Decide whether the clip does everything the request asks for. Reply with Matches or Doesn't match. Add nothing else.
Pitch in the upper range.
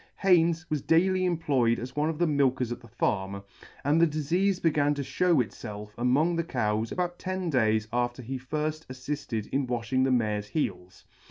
Doesn't match